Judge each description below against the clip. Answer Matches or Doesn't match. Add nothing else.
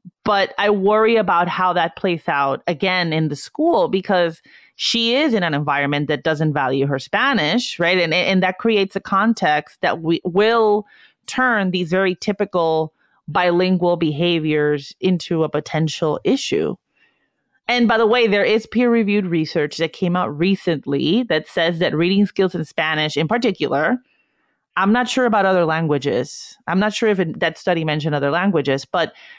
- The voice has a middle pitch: Matches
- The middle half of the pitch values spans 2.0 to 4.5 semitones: Doesn't match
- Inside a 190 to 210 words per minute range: Doesn't match